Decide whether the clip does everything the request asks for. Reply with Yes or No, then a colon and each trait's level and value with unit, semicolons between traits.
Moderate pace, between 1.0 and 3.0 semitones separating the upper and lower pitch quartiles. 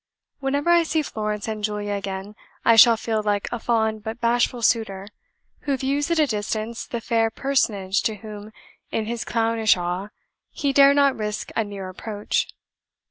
Yes: average, 170 wpm; average, 2.7 semitones